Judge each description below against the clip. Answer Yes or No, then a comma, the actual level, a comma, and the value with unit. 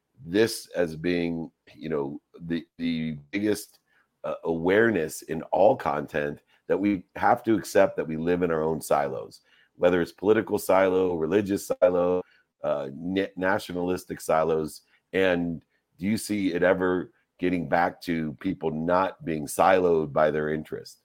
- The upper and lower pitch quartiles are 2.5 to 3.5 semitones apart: Yes, average, 2.8 semitones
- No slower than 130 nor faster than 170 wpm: Yes, average, 145 wpm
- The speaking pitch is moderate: No, very low, 90 Hz